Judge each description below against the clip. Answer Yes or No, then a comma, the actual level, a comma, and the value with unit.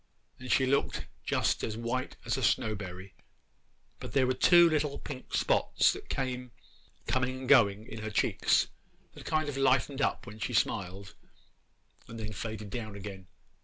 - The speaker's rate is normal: Yes, average, 165 wpm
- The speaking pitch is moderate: No, low, 120 Hz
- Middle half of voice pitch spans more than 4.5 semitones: No, average, 4.0 semitones